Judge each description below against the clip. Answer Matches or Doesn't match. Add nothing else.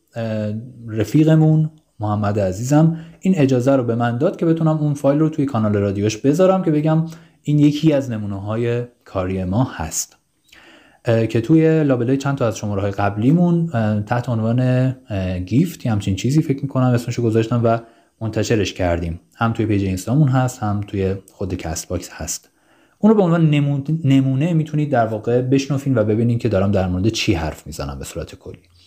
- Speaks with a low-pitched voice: Matches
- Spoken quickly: Doesn't match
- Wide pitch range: Matches